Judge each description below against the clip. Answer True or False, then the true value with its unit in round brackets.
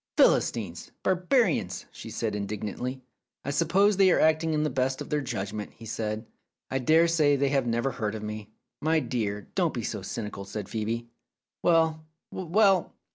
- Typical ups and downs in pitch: False (7.1 semitones)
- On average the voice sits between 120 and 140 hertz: True (135 Hz)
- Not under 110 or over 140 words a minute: False (175 wpm)